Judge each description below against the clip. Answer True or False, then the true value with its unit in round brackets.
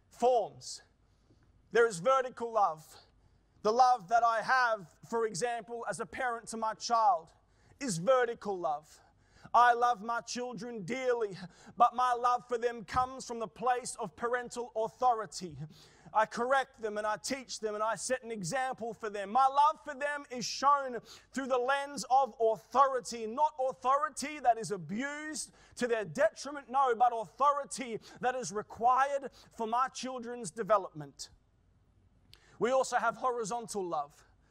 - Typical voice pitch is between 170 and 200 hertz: False (235 Hz)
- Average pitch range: True (3.4 semitones)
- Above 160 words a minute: False (150 wpm)